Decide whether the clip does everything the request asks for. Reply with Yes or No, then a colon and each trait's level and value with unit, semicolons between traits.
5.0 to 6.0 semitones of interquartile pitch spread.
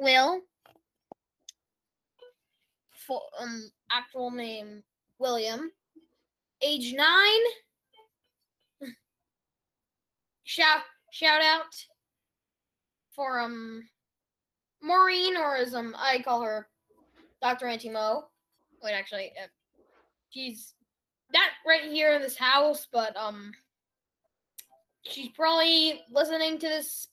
Yes: wide, 5.5 semitones